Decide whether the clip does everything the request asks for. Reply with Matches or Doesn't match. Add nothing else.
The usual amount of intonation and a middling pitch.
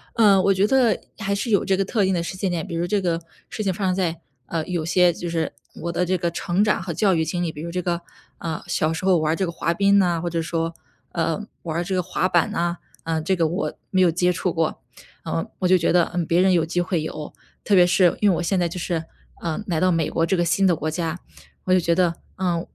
Doesn't match